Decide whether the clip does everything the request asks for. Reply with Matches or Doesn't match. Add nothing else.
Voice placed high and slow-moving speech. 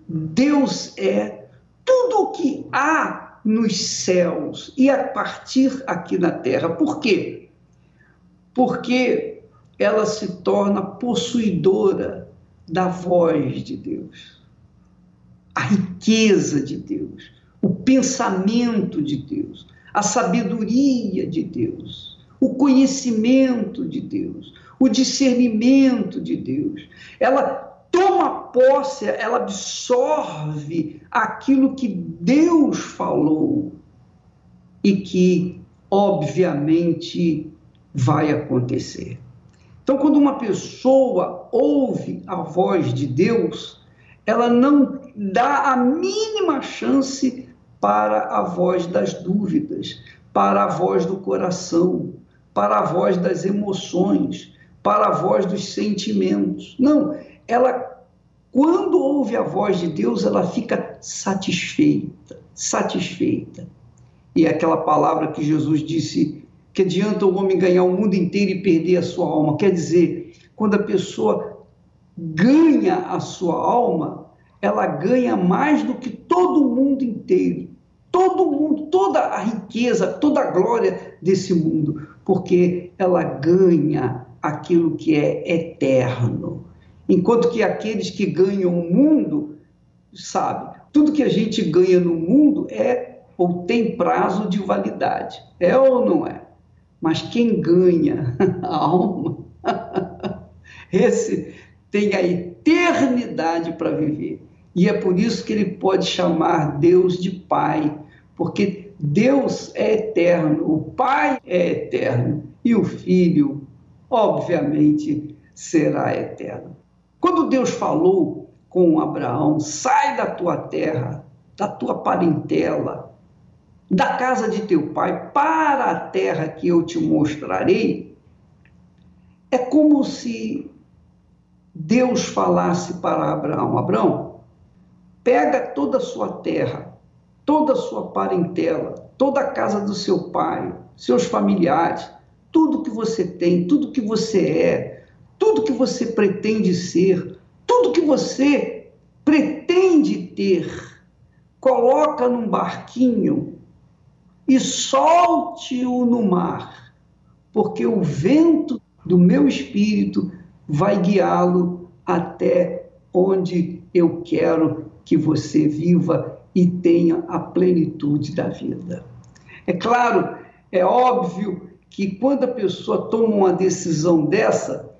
Matches